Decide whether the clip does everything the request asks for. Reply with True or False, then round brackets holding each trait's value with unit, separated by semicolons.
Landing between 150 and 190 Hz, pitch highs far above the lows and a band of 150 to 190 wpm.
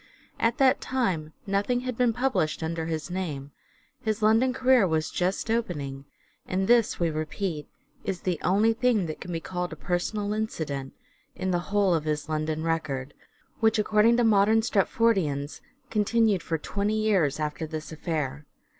True (185 Hz; 5.8 semitones; 160 wpm)